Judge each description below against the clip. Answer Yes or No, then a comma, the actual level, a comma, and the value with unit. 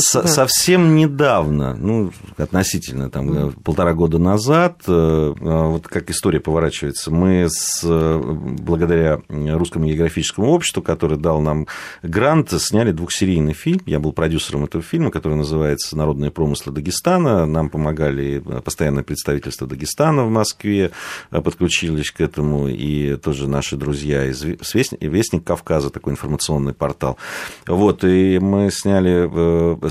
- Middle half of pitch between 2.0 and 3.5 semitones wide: No, average, 4.1 semitones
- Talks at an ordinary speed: Yes, average, 120 wpm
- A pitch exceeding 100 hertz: No, very low, 80 Hz